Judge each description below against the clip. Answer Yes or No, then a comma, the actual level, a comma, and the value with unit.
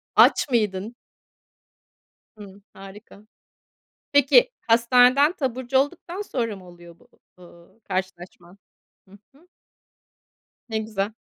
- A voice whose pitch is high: Yes, high, 220 Hz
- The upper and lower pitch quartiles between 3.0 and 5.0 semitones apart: No, wide, 5.6 semitones